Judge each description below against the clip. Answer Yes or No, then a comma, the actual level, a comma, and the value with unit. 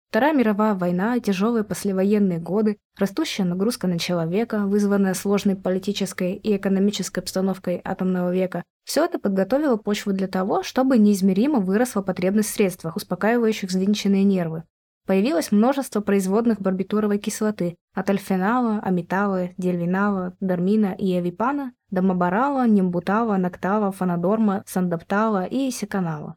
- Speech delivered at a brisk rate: No, average, 120 wpm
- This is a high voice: Yes, high, 200 Hz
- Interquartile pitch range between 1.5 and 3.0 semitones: Yes, narrow, 2.6 semitones